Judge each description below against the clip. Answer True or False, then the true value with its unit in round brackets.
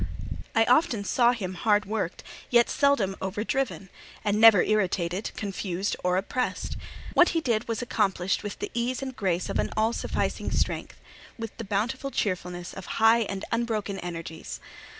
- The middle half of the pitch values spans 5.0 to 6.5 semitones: False (3.6 semitones)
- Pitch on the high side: True (210 Hz)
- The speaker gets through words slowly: False (155 wpm)